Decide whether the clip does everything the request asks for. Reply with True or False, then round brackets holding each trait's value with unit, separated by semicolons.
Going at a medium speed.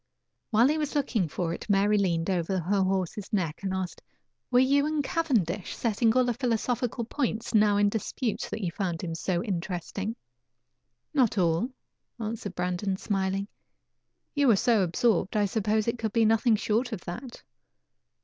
True (165 wpm)